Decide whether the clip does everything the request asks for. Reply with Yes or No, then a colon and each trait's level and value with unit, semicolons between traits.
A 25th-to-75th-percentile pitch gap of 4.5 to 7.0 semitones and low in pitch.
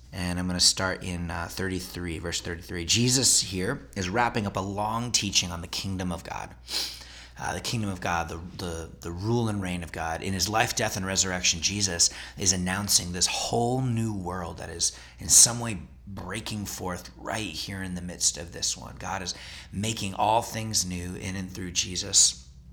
No: average, 3.1 semitones; very low, 90 Hz